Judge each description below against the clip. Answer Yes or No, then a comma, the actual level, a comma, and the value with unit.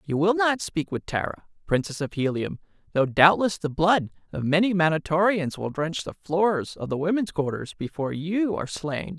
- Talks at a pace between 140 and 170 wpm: No, average, 185 wpm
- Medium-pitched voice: Yes, medium, 165 Hz